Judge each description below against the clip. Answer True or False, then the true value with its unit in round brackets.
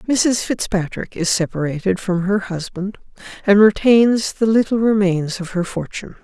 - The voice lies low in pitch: False (200 Hz)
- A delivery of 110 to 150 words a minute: True (145 wpm)